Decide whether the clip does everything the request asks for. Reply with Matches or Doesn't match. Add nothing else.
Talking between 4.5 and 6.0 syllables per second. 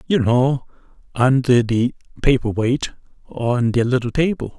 Doesn't match